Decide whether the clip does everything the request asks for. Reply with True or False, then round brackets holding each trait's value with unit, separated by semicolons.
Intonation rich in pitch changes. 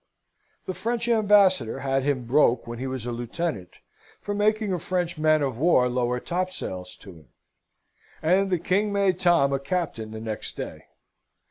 True (7.2 semitones)